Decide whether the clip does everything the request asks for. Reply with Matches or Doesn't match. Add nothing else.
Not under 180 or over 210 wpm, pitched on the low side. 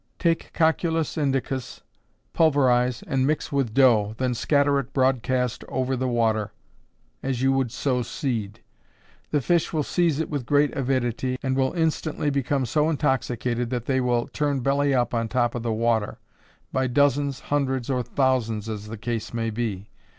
Doesn't match